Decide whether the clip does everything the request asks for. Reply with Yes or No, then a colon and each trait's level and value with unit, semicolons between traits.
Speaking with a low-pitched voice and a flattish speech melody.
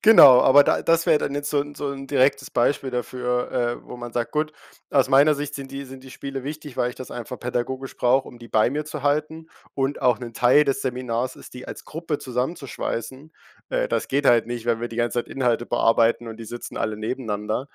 No: low, 130 Hz; average, 3.0 semitones